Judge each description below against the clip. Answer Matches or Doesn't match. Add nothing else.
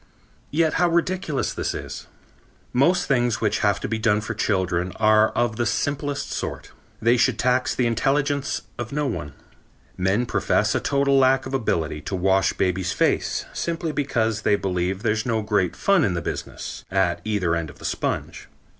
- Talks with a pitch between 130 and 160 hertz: Doesn't match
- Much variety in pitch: Matches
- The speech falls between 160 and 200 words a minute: Matches